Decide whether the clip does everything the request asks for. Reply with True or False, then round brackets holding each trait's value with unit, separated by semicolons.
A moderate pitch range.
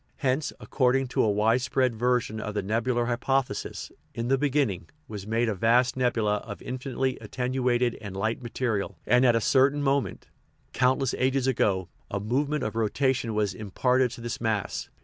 True (3.2 semitones)